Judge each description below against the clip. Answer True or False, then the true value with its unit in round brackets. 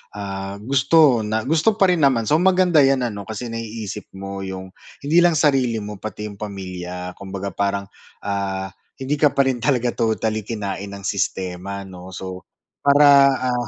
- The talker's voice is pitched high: False (110 Hz)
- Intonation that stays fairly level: False (5.8 semitones)